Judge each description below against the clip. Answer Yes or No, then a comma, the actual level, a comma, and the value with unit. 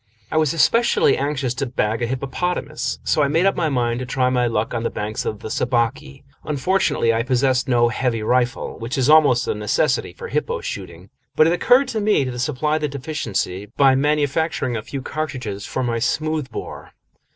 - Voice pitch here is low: Yes, low, 130 Hz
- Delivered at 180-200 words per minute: Yes, average, 190 wpm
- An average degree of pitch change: Yes, average, 4.3 semitones